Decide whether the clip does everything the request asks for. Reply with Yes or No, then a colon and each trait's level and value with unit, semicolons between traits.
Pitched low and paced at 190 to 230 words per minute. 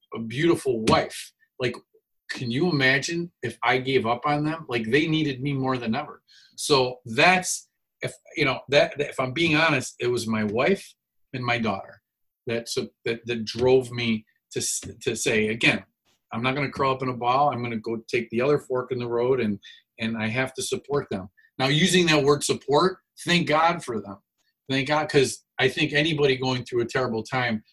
Yes: low, 130 Hz; fast, 205 wpm